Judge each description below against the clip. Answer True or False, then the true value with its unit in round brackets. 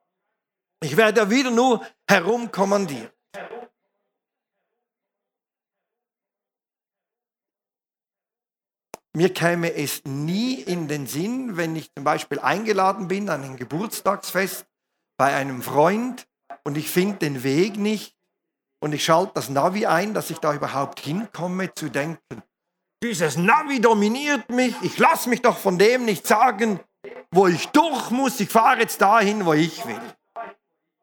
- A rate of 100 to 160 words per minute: True (130 wpm)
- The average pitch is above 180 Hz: True (190 Hz)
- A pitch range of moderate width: False (6.2 semitones)